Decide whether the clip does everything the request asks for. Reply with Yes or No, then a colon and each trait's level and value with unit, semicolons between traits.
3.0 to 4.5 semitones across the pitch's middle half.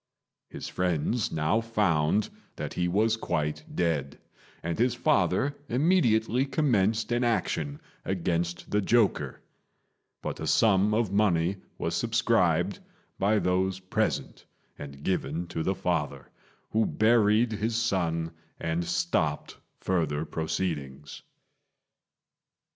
No: average, 5.2 semitones